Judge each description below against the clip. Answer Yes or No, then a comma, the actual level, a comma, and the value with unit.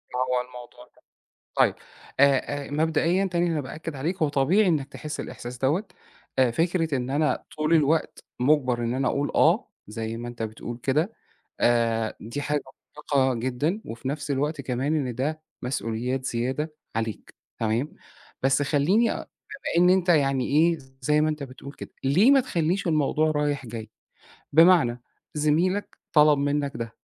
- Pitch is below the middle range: No, medium, 145 Hz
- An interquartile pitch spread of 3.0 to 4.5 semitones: Yes, average, 3.9 semitones